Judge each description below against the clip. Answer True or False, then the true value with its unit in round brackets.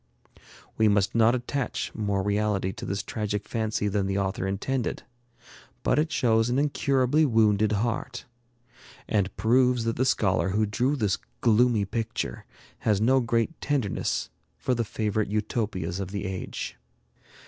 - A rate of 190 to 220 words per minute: False (150 wpm)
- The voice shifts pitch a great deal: False (3.3 semitones)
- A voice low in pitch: True (110 Hz)